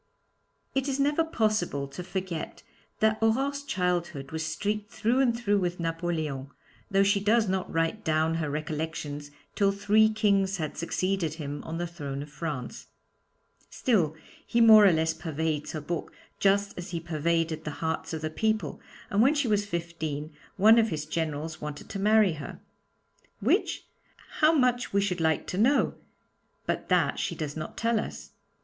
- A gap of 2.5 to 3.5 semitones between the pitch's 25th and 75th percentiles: No, average, 5.2 semitones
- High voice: No, medium, 175 Hz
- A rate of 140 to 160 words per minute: No, average, 170 wpm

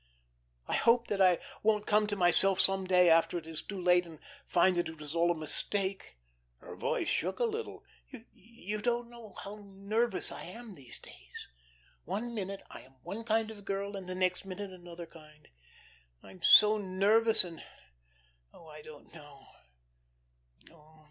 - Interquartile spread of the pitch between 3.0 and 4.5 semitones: Yes, average, 3.7 semitones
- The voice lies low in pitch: No, high, 190 Hz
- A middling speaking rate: Yes, average, 165 wpm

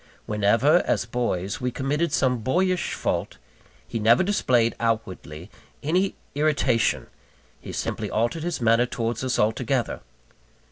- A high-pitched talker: No, low, 125 Hz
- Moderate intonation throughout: Yes, average, 4.7 semitones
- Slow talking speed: Yes, slow, 125 wpm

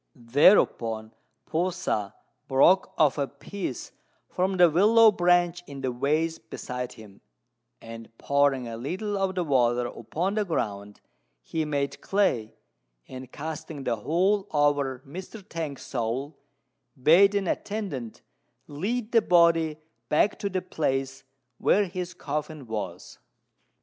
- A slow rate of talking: Yes, slow, 130 wpm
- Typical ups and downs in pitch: No, wide, 6.3 semitones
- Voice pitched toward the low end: No, medium, 150 Hz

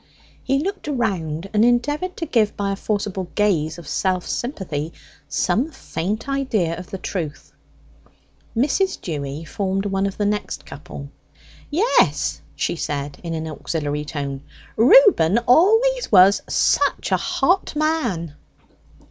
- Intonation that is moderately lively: No, wide, 9.0 semitones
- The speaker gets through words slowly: Yes, slow, 130 wpm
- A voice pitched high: Yes, high, 200 Hz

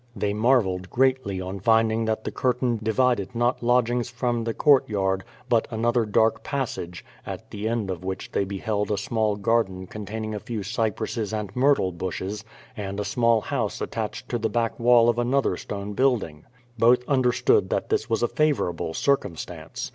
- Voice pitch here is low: Yes, low, 110 Hz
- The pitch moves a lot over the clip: No, average, 3.2 semitones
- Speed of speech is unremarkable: Yes, average, 170 wpm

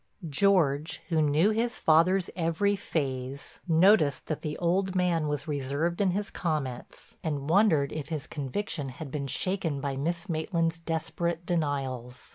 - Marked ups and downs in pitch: No, average, 3.8 semitones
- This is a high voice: No, medium, 160 Hz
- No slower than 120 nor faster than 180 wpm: Yes, average, 145 wpm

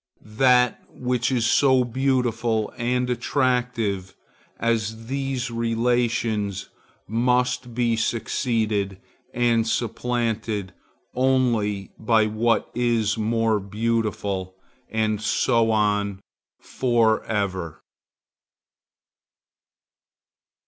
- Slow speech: Yes, slow, 75 wpm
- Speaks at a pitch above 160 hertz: No, low, 115 Hz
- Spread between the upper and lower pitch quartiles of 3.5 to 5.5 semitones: No, narrow, 2.4 semitones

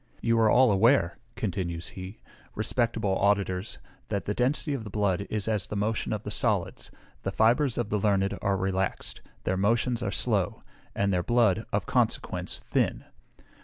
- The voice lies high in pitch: No, low, 105 Hz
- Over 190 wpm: No, average, 165 wpm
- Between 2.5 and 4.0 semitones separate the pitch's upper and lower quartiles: Yes, average, 3.1 semitones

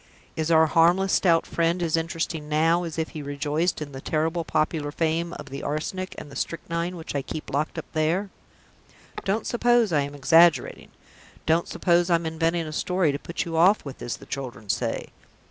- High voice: No, medium, 165 Hz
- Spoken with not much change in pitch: Yes, narrow, 2.2 semitones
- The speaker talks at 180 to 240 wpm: Yes, average, 190 wpm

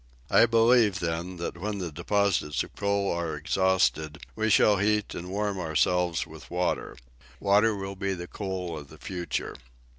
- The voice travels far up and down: No, average, 2.9 semitones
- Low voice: Yes, very low, 95 Hz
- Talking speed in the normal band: Yes, average, 160 wpm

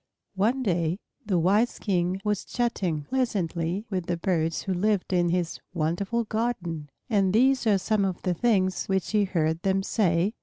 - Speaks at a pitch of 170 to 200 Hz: Yes, high, 190 Hz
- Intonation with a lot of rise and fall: No, average, 3.7 semitones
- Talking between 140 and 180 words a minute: Yes, average, 165 wpm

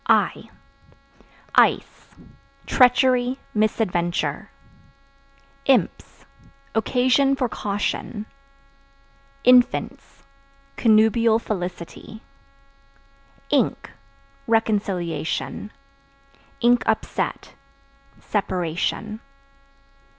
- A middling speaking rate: No, slow, 45 wpm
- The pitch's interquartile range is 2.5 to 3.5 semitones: No, average, 3.9 semitones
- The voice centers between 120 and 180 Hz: No, high, 220 Hz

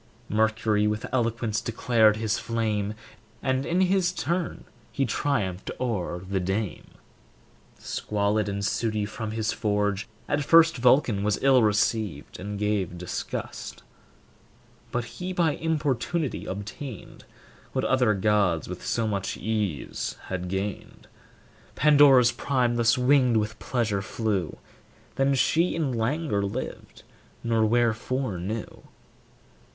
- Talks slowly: Yes, slow, 120 wpm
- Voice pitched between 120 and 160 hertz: No, low, 110 Hz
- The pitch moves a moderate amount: Yes, average, 4.1 semitones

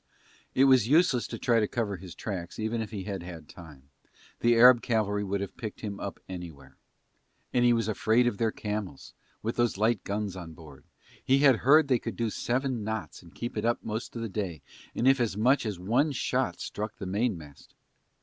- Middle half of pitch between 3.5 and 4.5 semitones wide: Yes, average, 4.0 semitones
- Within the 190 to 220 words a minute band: Yes, fast, 205 wpm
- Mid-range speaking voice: No, low, 110 Hz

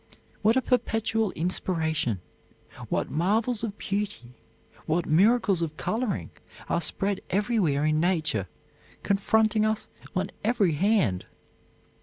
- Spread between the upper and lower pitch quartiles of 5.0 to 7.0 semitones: Yes, wide, 5.6 semitones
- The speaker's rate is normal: No, slow, 110 wpm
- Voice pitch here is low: No, high, 195 Hz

